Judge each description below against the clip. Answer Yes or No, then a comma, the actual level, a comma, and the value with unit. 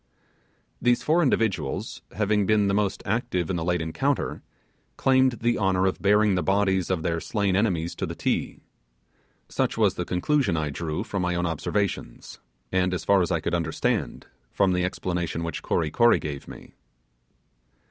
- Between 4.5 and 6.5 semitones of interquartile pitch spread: No, average, 3.7 semitones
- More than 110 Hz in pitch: No, very low, 95 Hz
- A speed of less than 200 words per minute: Yes, average, 170 wpm